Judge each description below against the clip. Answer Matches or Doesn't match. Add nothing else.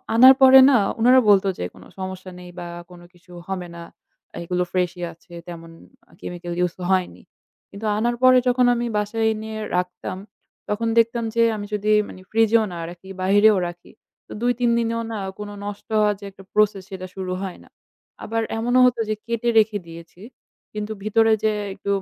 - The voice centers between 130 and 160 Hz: Doesn't match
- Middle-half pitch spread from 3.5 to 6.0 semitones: Matches